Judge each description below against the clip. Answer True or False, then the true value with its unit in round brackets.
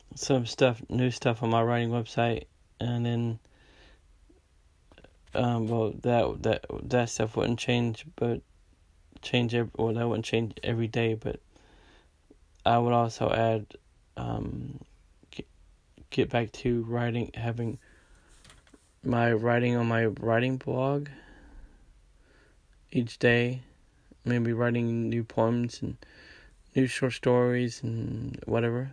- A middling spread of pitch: False (1.5 semitones)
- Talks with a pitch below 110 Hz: False (120 Hz)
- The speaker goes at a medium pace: False (115 wpm)